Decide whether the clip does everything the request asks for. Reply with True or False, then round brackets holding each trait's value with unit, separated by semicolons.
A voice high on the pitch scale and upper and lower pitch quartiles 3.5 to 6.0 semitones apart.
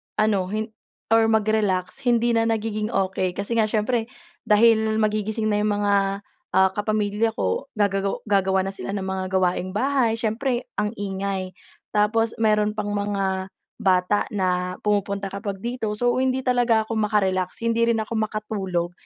False (210 Hz; 2.5 semitones)